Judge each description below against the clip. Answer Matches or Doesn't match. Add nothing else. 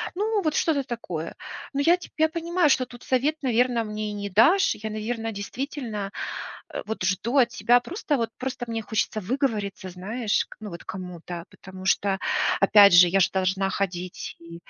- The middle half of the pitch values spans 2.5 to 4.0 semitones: Doesn't match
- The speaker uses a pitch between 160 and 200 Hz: Doesn't match